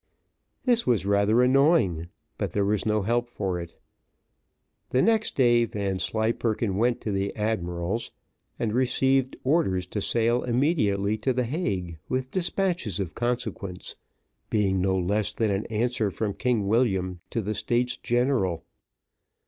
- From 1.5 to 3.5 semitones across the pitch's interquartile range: No, average, 4.1 semitones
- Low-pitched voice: Yes, low, 110 Hz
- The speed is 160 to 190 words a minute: No, average, 140 wpm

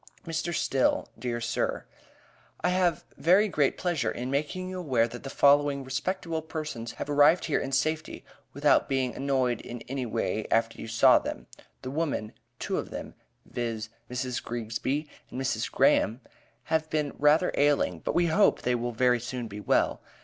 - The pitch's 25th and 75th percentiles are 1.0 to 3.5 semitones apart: No, average, 4.5 semitones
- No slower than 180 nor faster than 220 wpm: No, average, 170 wpm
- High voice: No, low, 135 Hz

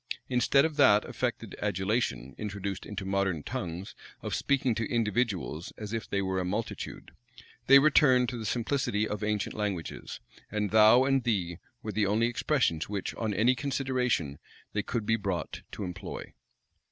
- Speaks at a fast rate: No, average, 160 wpm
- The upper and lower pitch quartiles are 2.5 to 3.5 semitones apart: No, average, 4.1 semitones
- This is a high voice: No, low, 105 Hz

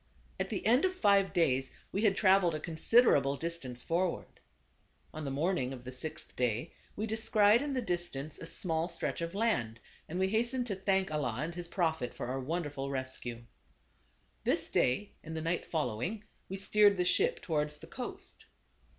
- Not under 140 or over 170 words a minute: No, average, 180 wpm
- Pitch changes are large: Yes, wide, 6.4 semitones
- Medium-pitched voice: Yes, medium, 170 Hz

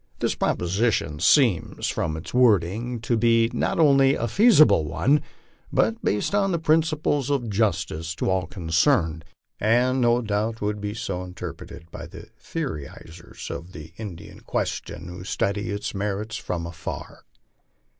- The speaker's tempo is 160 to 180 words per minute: No, average, 140 wpm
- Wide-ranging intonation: Yes, wide, 6.1 semitones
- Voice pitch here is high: No, low, 105 Hz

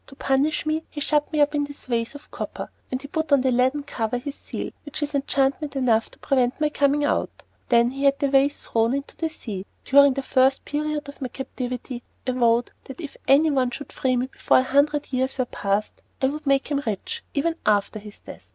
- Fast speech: Yes, fast, 225 wpm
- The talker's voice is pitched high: Yes, very high, 275 Hz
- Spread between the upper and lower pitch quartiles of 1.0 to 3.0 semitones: Yes, narrow, 2.5 semitones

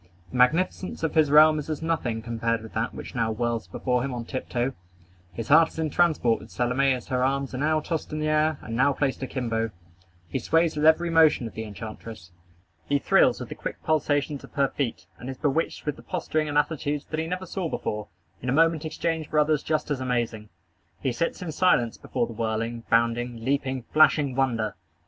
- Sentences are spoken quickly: Yes, fast, 210 wpm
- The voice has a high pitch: No, low, 135 Hz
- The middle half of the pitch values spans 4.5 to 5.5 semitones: Yes, average, 4.8 semitones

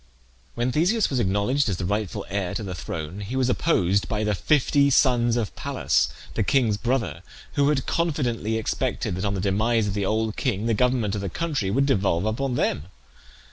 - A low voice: Yes, low, 110 Hz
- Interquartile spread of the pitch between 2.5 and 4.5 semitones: No, average, 4.9 semitones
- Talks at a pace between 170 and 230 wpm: Yes, average, 195 wpm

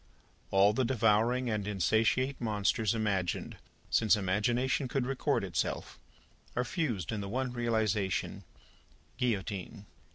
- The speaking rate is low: Yes, slow, 110 wpm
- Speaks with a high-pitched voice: No, low, 110 Hz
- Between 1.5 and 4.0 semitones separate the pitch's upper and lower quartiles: Yes, average, 3.5 semitones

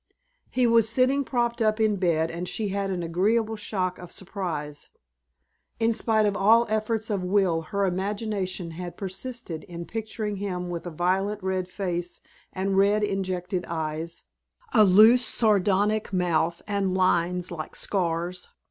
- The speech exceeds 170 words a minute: No, average, 150 wpm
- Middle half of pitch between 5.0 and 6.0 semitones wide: No, average, 3.3 semitones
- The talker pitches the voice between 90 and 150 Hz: No, high, 195 Hz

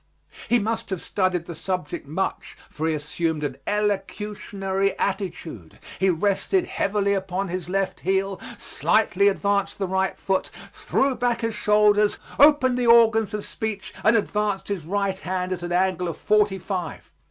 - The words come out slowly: No, average, 155 wpm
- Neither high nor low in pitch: No, high, 195 Hz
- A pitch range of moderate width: No, narrow, 2.3 semitones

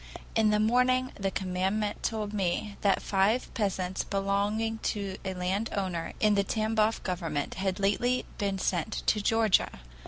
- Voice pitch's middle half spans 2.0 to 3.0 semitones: Yes, narrow, 2.4 semitones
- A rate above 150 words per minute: No, average, 145 wpm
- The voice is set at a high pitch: Yes, high, 200 Hz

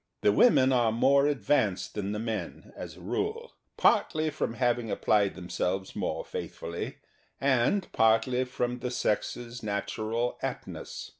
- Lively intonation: No, average, 4.0 semitones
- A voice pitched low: Yes, low, 115 Hz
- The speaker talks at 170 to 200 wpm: No, average, 140 wpm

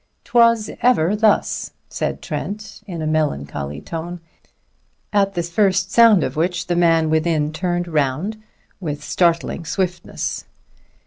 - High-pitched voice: No, medium, 175 Hz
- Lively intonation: No, average, 4.0 semitones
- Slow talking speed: Yes, slow, 125 wpm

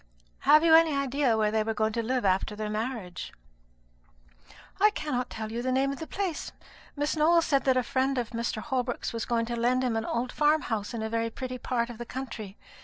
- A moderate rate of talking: No, fast, 225 wpm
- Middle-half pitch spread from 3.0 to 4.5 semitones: Yes, average, 3.6 semitones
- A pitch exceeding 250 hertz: No, high, 245 Hz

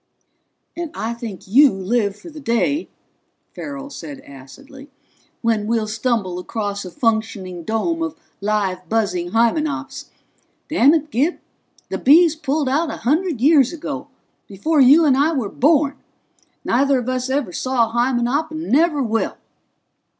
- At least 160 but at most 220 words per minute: No, average, 145 wpm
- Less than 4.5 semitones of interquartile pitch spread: No, average, 5.3 semitones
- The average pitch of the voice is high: Yes, very high, 255 Hz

